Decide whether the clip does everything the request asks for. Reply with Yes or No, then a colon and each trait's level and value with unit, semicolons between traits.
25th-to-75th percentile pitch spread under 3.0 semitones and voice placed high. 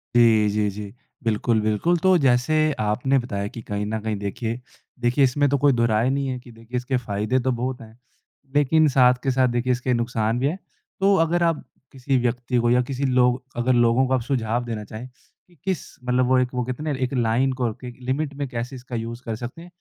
No: narrow, 2.5 semitones; low, 125 Hz